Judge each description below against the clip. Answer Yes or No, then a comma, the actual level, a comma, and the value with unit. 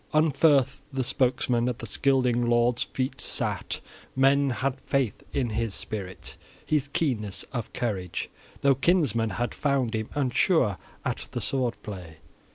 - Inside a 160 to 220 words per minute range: No, average, 140 wpm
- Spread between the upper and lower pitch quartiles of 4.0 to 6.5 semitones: No, average, 3.4 semitones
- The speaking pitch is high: No, low, 125 Hz